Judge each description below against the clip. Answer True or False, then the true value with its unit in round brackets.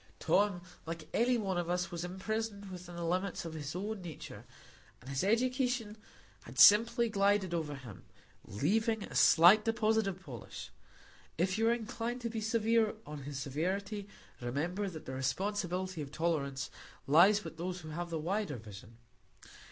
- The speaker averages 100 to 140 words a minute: False (160 wpm)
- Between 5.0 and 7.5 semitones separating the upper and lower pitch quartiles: True (5.3 semitones)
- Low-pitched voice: False (185 Hz)